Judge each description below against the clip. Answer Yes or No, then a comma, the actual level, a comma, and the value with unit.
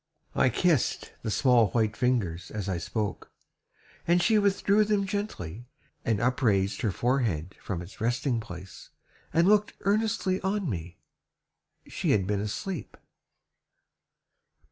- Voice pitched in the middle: No, low, 120 Hz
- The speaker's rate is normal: No, slow, 125 wpm